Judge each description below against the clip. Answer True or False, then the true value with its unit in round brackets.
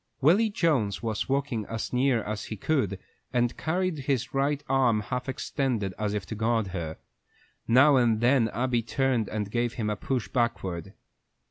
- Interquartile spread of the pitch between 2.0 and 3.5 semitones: False (4.0 semitones)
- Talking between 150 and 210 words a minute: True (170 wpm)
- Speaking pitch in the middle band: False (120 Hz)